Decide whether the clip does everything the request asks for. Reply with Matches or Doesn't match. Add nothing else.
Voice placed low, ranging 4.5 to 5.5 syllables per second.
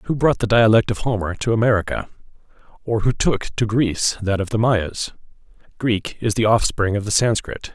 Matches